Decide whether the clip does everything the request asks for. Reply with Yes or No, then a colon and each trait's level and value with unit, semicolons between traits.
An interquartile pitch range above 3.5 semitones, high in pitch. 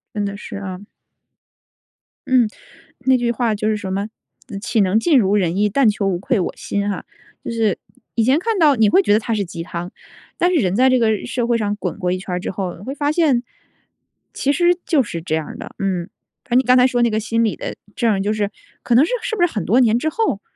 Yes: average, 4.3 semitones; high, 220 Hz